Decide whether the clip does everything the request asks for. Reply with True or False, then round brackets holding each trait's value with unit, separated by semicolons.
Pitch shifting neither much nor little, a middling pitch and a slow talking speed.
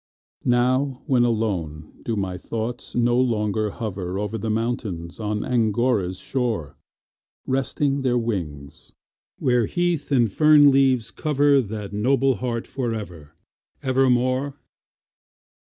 False (4.1 semitones; 120 Hz; 120 wpm)